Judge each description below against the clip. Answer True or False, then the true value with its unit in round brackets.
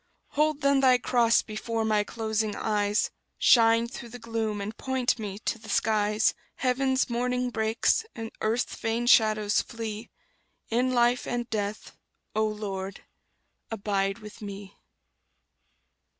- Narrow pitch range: True (2.3 semitones)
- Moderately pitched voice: False (225 Hz)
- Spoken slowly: True (130 wpm)